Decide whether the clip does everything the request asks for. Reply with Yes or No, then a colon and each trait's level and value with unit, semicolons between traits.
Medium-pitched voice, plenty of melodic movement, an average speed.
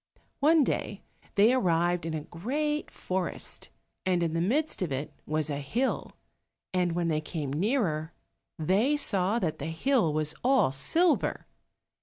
Yes: medium, 175 Hz; wide, 8.3 semitones; average, 150 wpm